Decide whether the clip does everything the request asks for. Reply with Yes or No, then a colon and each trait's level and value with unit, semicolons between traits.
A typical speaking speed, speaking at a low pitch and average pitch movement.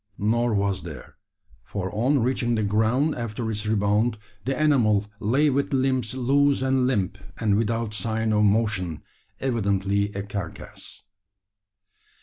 No: slow, 130 wpm; low, 110 Hz; average, 4.0 semitones